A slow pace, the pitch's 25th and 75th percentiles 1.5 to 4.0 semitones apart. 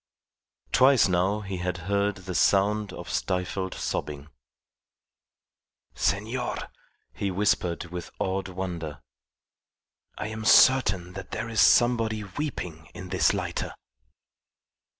Yes: slow, 110 wpm; average, 3.0 semitones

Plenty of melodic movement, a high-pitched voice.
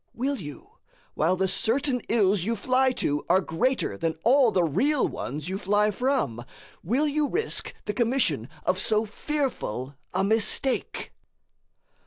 Yes: wide, 7.0 semitones; high, 215 Hz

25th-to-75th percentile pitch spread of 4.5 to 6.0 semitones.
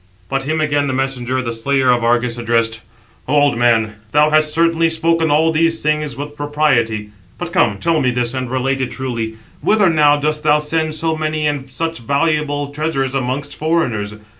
No: average, 3.8 semitones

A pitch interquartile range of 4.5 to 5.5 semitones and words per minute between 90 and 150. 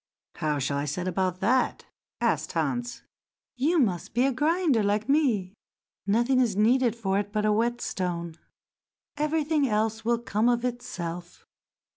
Yes: average, 4.8 semitones; average, 140 wpm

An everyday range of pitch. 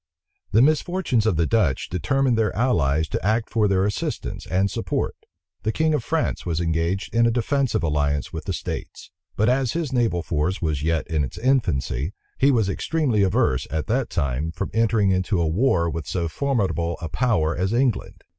No: wide, 6.7 semitones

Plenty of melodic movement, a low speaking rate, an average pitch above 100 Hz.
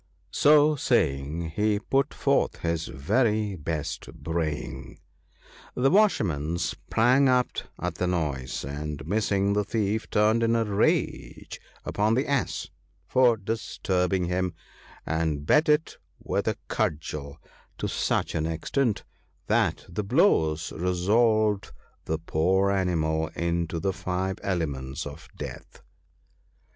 No: wide, 5.7 semitones; slow, 120 wpm; very low, 95 Hz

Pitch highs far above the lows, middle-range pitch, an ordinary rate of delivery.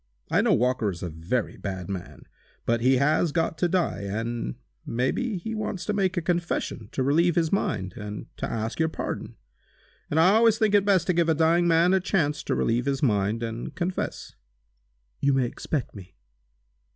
Yes: wide, 7.5 semitones; medium, 150 Hz; average, 195 wpm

